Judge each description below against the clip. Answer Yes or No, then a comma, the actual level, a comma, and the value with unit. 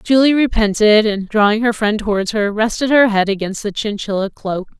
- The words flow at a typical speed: Yes, average, 190 wpm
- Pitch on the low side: No, high, 215 Hz